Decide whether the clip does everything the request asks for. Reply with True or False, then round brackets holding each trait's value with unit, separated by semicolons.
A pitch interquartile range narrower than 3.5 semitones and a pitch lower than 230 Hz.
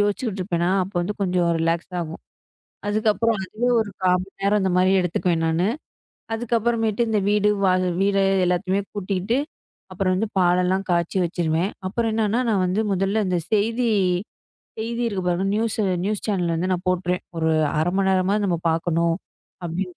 True (3.0 semitones; 190 Hz)